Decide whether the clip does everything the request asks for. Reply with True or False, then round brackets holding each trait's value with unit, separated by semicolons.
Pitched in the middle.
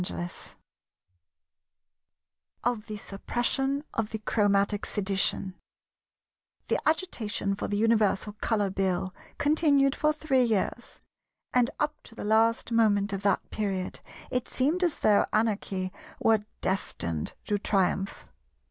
False (215 Hz)